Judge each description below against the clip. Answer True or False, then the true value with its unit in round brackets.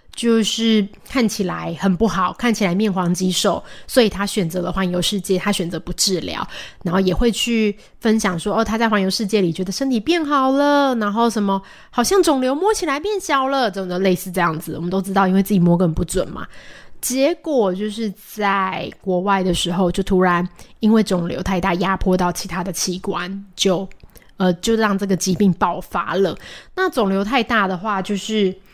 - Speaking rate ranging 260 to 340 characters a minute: True (285 characters per minute)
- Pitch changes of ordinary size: True (3.4 semitones)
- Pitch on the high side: True (195 Hz)